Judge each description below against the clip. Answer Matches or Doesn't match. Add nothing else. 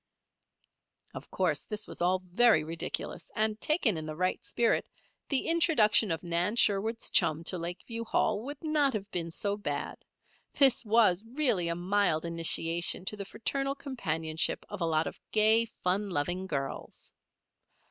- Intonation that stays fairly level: Doesn't match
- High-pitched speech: Matches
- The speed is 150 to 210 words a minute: Matches